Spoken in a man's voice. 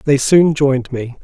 Yes: male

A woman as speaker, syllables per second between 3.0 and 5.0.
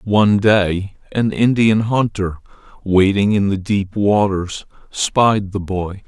No: male; 3.5 syllables/s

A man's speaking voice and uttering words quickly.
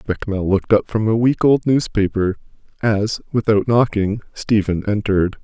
No: male; average, 145 wpm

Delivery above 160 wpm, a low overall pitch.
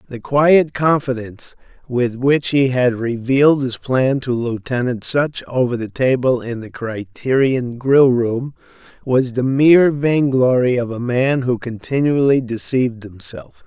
No: average, 140 wpm; low, 130 Hz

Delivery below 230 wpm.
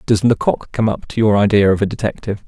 No: fast, 240 wpm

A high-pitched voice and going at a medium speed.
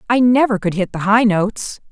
No: high, 215 Hz; fast, 220 wpm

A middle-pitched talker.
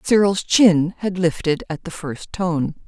Yes: medium, 175 Hz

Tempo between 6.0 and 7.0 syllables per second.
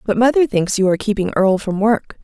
Yes: 6.3 syllables/s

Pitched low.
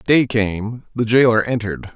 Yes: low, 115 Hz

